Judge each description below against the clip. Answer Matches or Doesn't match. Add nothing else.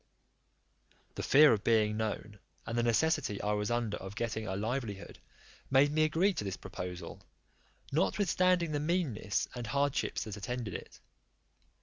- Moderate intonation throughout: Doesn't match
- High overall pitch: Doesn't match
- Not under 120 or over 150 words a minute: Matches